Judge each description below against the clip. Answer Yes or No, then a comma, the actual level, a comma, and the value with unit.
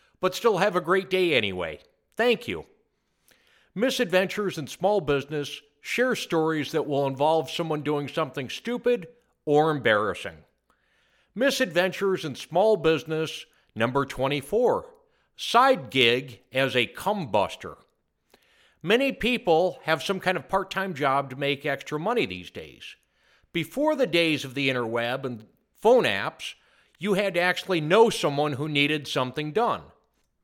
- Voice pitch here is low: No, medium, 160 Hz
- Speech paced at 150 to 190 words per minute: No, slow, 135 wpm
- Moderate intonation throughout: No, wide, 6.1 semitones